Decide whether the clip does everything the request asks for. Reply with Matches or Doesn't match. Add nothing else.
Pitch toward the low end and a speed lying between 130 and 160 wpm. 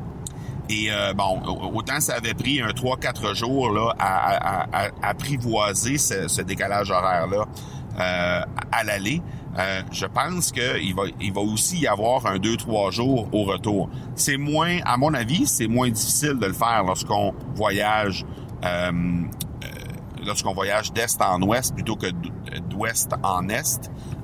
Matches